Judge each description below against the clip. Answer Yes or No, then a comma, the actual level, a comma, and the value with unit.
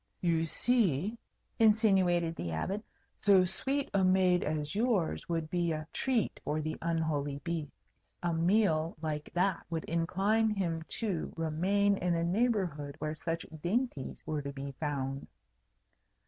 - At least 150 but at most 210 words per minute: No, average, 140 wpm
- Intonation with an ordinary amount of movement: Yes, average, 4.2 semitones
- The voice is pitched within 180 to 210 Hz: No, medium, 170 Hz